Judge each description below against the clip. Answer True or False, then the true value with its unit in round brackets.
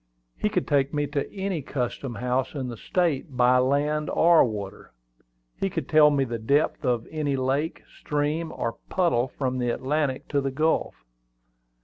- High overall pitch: False (140 Hz)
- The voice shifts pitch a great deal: False (3.3 semitones)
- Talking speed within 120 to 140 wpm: False (165 wpm)